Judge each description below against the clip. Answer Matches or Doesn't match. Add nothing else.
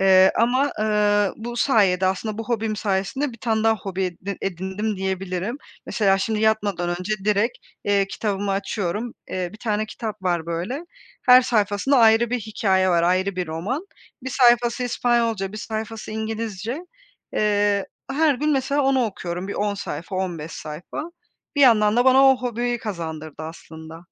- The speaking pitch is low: Doesn't match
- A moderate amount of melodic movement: Matches